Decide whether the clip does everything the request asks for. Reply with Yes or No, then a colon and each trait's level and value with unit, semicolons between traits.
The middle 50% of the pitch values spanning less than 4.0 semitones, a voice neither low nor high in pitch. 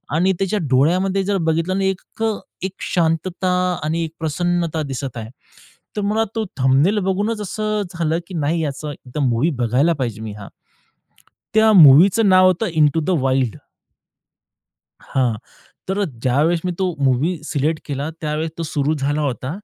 No: average, 5.0 semitones; medium, 160 Hz